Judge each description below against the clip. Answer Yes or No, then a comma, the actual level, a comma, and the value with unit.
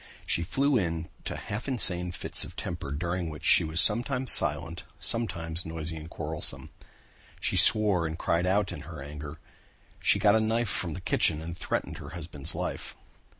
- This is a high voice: No, very low, 85 Hz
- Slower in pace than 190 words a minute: Yes, average, 170 wpm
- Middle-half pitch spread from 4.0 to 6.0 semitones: Yes, average, 4.3 semitones